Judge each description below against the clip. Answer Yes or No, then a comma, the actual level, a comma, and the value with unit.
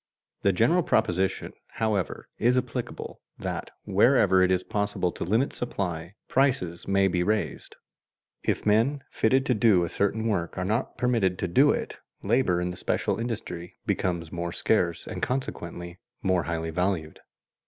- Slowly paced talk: No, average, 155 wpm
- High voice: No, very low, 95 Hz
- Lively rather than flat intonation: No, average, 4.5 semitones